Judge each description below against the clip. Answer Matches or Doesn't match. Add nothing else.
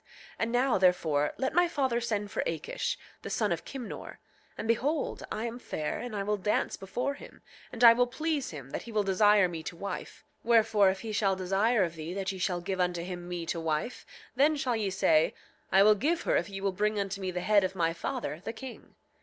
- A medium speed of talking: Doesn't match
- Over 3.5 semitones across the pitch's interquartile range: Matches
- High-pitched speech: Matches